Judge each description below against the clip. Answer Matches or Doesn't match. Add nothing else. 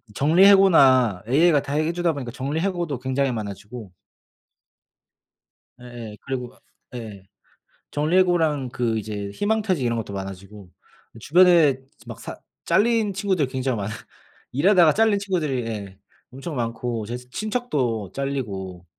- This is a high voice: Doesn't match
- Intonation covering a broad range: Matches